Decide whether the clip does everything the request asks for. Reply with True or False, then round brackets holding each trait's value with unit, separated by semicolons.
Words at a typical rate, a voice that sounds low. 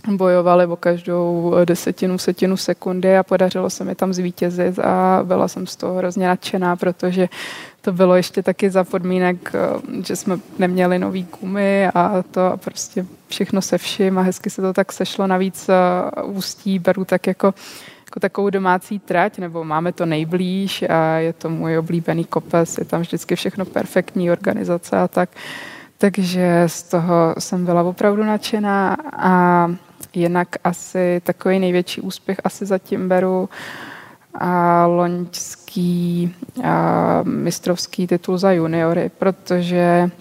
False (140 wpm; 180 Hz)